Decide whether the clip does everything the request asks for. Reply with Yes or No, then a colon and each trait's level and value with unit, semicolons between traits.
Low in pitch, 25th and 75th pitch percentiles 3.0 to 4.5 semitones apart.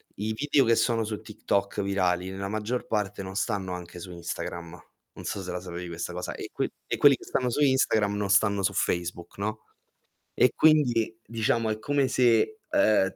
Yes: low, 105 Hz; average, 3.8 semitones